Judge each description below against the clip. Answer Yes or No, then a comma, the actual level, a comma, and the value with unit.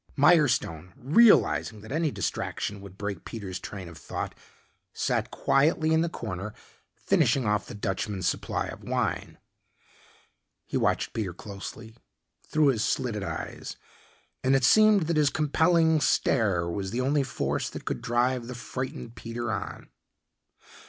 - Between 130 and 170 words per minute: Yes, average, 140 wpm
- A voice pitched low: Yes, low, 120 Hz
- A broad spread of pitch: Yes, wide, 6.3 semitones